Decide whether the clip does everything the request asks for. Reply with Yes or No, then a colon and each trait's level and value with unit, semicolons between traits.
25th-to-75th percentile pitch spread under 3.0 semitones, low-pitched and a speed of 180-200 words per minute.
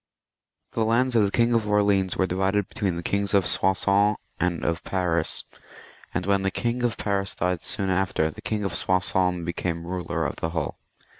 Yes: narrow, 2.5 semitones; very low, 95 Hz; average, 190 wpm